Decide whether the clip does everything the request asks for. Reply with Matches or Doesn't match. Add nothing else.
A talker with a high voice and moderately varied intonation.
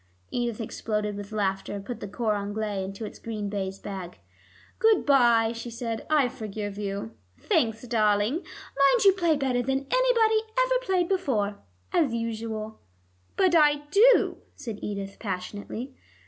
Doesn't match